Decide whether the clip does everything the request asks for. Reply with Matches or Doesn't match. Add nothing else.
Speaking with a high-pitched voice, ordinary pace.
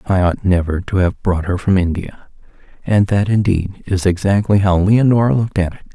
Doesn't match